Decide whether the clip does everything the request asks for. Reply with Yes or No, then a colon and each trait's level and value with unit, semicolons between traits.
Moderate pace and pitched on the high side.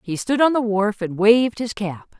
No: fast, 245 wpm; high, 215 Hz